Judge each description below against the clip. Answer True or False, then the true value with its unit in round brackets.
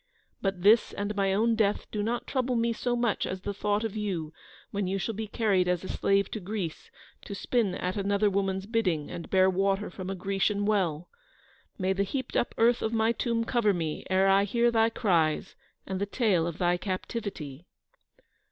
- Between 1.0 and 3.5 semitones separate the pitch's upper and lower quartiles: True (3.0 semitones)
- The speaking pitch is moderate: False (200 Hz)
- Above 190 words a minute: True (200 wpm)